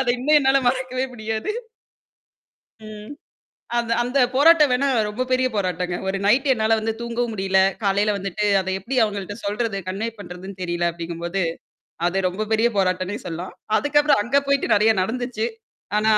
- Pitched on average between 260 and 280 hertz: No, high, 215 Hz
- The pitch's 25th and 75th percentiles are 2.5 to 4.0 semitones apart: No, average, 4.6 semitones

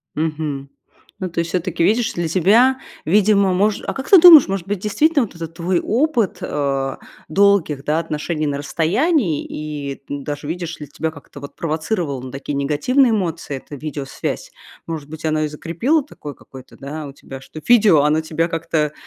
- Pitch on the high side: No, medium, 160 Hz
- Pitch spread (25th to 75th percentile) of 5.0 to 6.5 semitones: Yes, average, 5.3 semitones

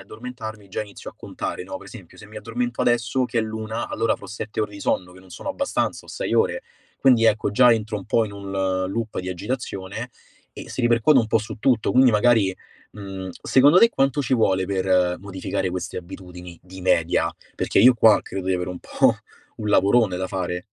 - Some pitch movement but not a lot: Yes, average, 3.9 semitones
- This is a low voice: Yes, low, 105 Hz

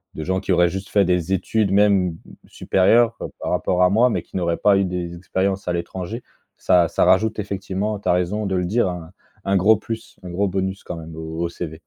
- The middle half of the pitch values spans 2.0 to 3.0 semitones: Yes, narrow, 2.5 semitones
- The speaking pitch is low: Yes, very low, 95 Hz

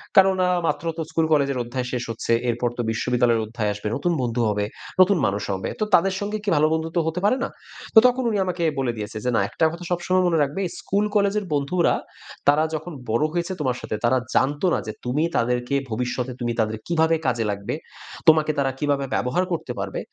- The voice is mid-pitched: Yes, medium, 145 Hz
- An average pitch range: No, wide, 6.2 semitones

